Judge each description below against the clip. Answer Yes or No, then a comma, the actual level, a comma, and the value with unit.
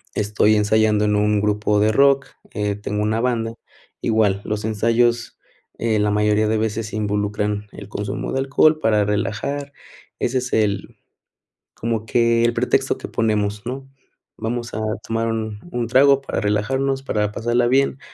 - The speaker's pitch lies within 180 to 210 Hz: No, low, 110 Hz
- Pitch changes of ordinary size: No, narrow, 2.3 semitones